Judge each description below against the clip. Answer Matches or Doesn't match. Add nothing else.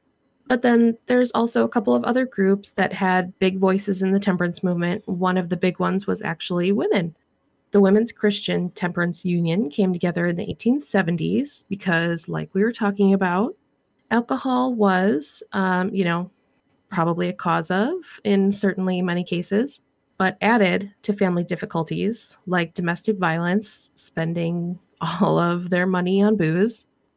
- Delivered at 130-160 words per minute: Matches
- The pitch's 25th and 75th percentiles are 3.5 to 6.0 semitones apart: Doesn't match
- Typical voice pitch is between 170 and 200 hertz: Matches